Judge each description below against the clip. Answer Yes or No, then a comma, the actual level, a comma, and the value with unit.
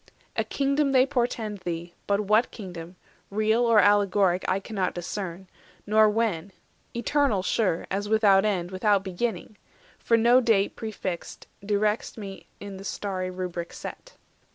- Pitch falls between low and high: No, high, 205 Hz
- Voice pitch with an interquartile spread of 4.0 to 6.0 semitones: No, average, 3.0 semitones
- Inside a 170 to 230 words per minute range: No, average, 140 wpm